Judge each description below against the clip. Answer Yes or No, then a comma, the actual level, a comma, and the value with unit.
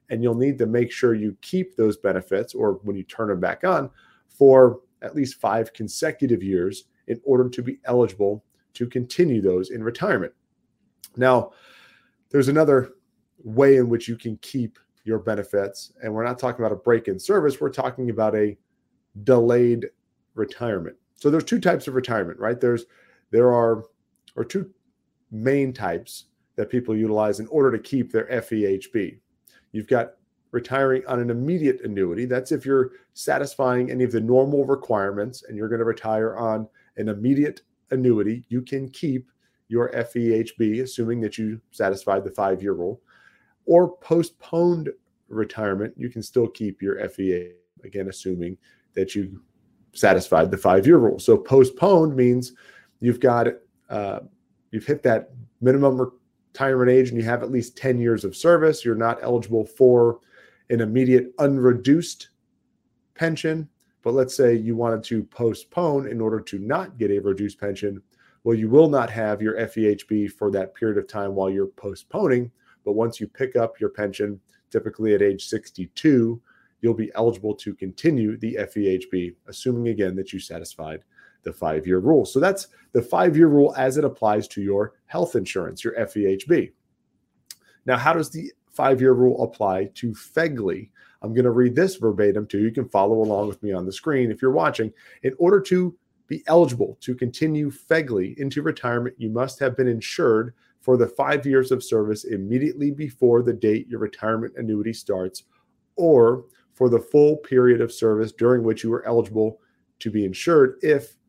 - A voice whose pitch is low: Yes, low, 120 Hz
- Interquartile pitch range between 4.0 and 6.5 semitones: No, average, 3.5 semitones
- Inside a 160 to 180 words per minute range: Yes, average, 170 wpm